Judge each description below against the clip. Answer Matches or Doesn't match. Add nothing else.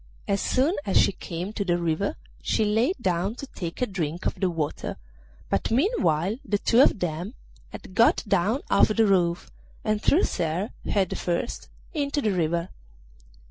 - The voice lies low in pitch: Doesn't match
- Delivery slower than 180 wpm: Matches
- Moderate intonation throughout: Matches